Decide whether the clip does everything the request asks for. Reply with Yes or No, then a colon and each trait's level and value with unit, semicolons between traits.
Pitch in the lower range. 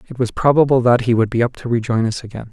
Yes: low, 120 Hz